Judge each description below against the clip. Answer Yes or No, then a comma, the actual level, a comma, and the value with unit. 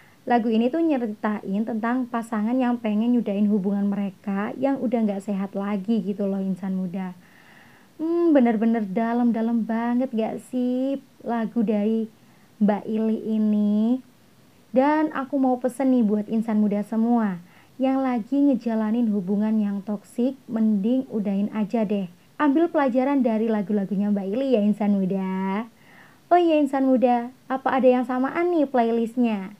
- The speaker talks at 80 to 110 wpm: No, fast, 140 wpm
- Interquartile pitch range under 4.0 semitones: Yes, average, 3.5 semitones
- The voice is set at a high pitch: Yes, high, 225 Hz